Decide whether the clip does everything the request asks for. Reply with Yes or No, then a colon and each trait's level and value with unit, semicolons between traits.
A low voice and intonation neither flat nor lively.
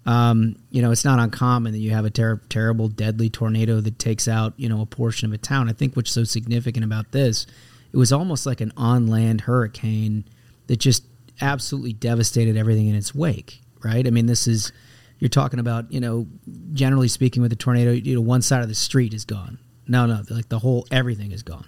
No: low, 120 Hz; narrow, 2.0 semitones